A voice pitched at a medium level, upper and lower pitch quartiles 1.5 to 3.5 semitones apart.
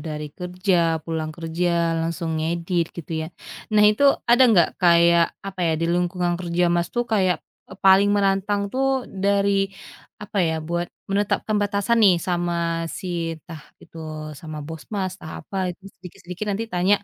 Yes: medium, 180 Hz; average, 2.8 semitones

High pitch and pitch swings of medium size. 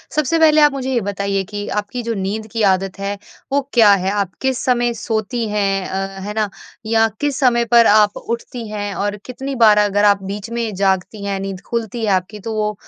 Yes: high, 210 Hz; average, 3.0 semitones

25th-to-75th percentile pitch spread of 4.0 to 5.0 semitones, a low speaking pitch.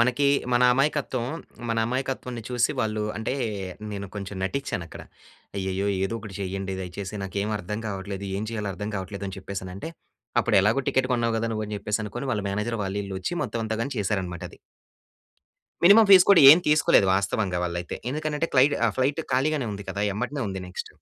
Yes: average, 4.7 semitones; low, 105 Hz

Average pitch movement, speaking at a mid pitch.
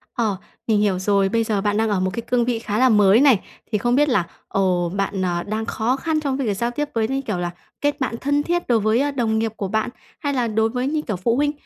No: average, 4.3 semitones; high, 225 Hz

